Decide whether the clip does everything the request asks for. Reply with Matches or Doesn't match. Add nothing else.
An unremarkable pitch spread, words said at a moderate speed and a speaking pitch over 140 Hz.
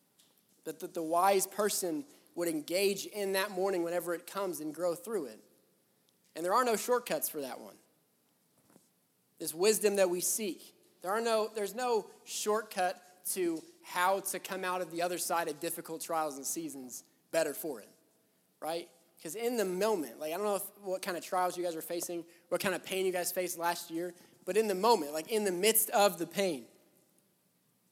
Matches